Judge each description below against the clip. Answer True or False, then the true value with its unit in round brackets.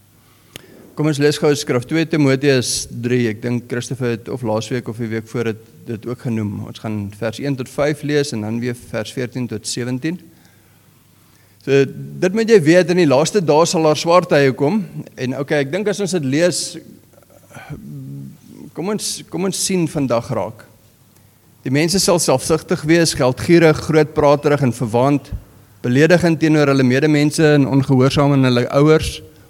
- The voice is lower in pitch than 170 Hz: True (140 Hz)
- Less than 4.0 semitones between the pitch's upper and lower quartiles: False (4.9 semitones)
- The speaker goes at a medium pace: True (165 wpm)